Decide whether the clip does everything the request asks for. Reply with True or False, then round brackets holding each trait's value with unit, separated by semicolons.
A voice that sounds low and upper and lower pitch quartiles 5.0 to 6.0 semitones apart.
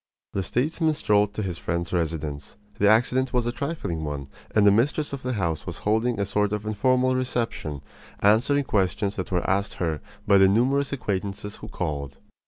True (105 Hz; 5.5 semitones)